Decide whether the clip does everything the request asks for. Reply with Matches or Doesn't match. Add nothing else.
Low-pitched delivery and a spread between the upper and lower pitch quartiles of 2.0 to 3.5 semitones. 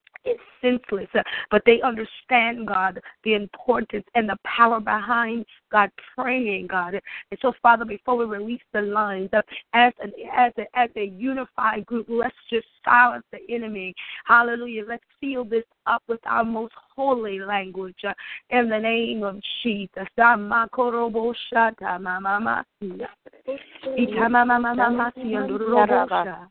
Doesn't match